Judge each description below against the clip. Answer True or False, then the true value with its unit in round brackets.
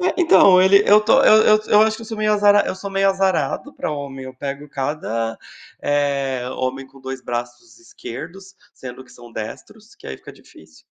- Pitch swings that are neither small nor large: False (7.8 semitones)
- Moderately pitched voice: True (150 Hz)